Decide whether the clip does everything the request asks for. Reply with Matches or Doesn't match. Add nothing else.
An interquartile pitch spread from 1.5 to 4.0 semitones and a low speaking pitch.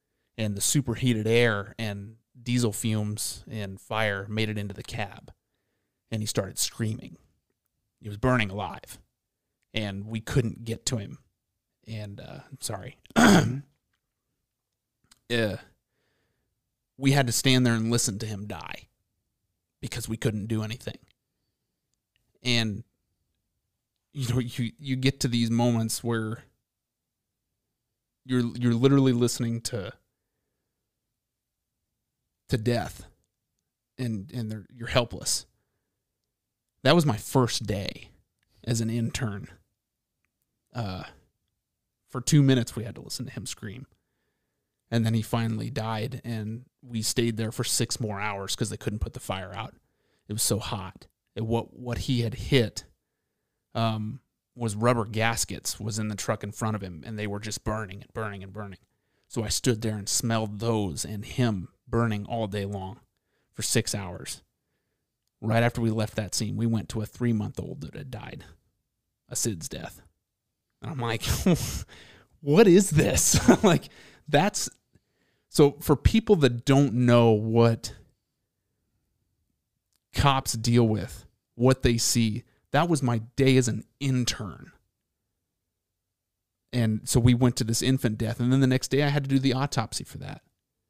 Matches